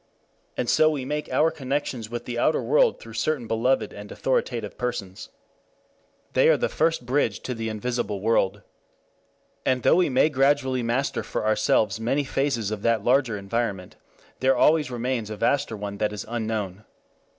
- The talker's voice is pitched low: Yes, low, 120 Hz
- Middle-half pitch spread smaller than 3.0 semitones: No, average, 3.9 semitones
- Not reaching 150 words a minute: No, average, 165 wpm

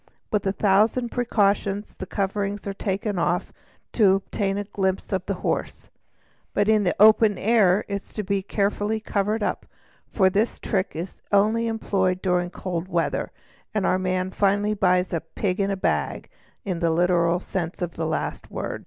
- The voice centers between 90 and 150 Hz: No, high, 195 Hz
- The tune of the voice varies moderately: No, narrow, 2.1 semitones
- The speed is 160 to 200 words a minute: Yes, average, 170 wpm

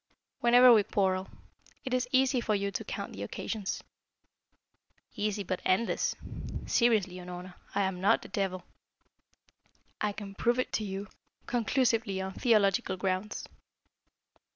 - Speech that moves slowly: Yes, slow, 130 wpm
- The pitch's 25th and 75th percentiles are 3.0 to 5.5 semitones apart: Yes, average, 3.8 semitones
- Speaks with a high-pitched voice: Yes, high, 205 Hz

